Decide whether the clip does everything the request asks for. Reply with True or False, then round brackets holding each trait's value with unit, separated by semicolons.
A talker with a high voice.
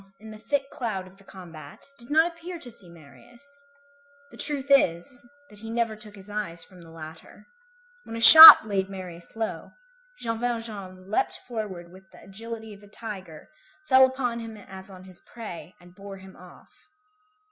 True (210 Hz)